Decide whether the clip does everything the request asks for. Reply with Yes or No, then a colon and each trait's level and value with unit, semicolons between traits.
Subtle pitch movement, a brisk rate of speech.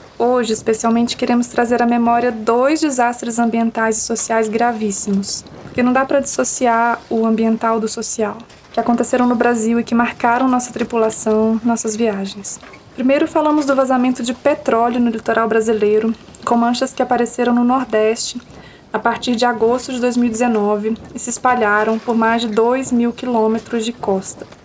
No: narrow, 1.5 semitones; average, 155 wpm